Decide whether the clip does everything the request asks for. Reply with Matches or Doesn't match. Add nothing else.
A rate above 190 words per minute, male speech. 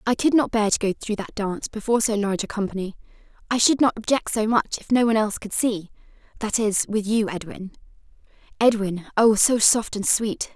Doesn't match